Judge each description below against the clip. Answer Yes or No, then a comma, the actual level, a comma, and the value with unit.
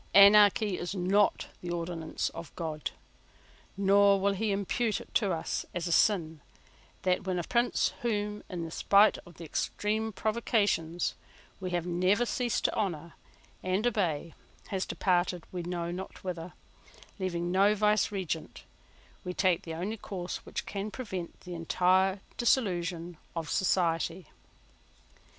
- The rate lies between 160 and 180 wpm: No, slow, 135 wpm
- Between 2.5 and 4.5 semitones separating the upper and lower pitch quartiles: Yes, average, 3.0 semitones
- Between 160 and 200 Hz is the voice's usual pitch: Yes, medium, 185 Hz